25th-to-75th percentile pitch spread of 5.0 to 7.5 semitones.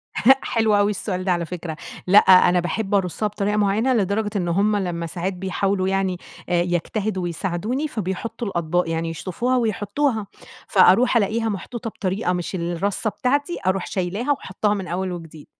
No: average, 3.4 semitones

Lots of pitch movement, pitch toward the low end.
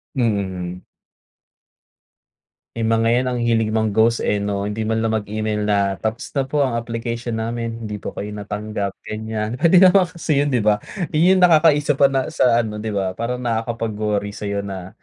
No: narrow, 2.5 semitones; low, 110 Hz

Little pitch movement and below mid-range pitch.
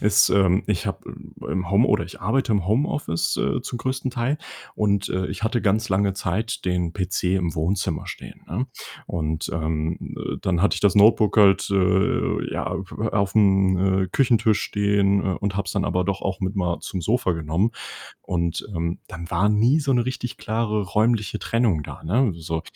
No: average, 3.3 semitones; low, 100 Hz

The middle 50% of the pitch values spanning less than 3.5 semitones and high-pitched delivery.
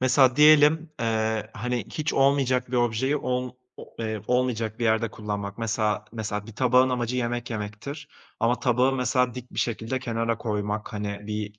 No: average, 2.7 semitones; low, 120 Hz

